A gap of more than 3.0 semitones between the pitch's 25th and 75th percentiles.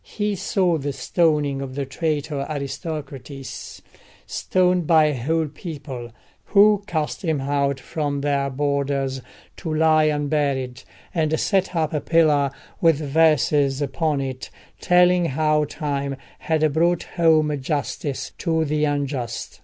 No: narrow, 2.6 semitones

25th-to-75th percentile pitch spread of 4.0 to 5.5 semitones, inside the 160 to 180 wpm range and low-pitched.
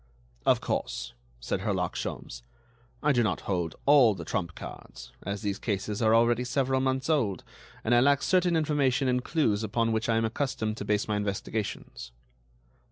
Yes: average, 4.3 semitones; average, 170 wpm; low, 115 Hz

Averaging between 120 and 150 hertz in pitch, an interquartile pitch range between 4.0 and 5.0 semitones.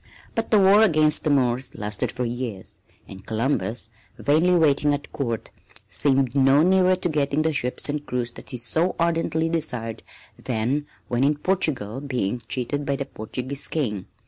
Yes: medium, 140 Hz; average, 4.3 semitones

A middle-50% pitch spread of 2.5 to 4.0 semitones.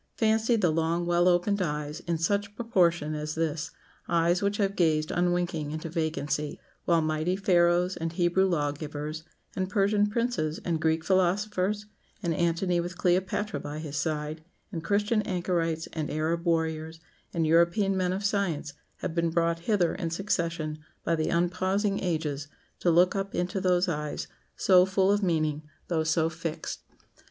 Yes: average, 3.0 semitones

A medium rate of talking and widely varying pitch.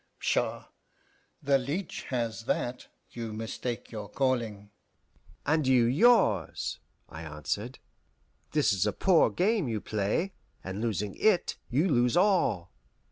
No: slow, 125 wpm; wide, 6.1 semitones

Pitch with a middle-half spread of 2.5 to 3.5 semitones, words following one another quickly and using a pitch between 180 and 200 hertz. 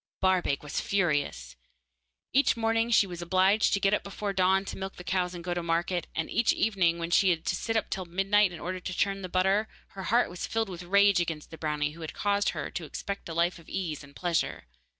Yes: average, 2.8 semitones; fast, 240 wpm; medium, 185 Hz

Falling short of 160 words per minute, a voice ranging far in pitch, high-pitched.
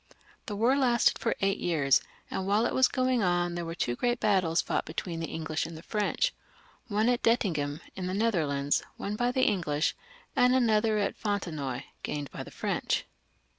No: average, 190 wpm; wide, 6.0 semitones; high, 195 Hz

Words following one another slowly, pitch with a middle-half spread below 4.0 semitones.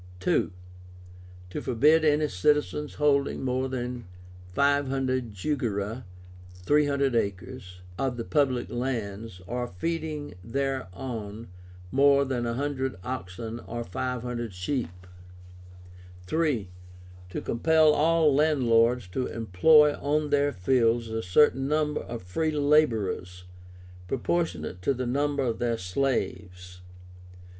No: slow, 105 wpm; average, 4.5 semitones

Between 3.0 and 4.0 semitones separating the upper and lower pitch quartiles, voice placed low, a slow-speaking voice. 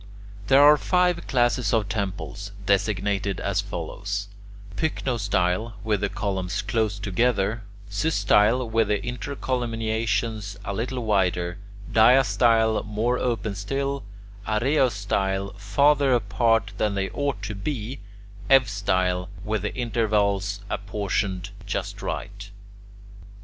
Yes: average, 3.3 semitones; low, 105 Hz; slow, 105 wpm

